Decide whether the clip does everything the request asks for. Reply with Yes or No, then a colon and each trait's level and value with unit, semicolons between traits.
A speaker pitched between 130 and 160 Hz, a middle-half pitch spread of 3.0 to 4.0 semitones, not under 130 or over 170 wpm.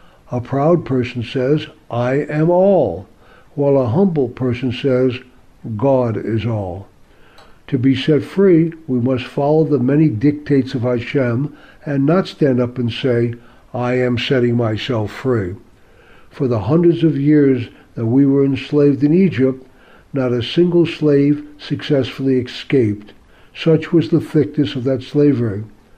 Yes: low, 135 Hz; average, 3.4 semitones; average, 145 wpm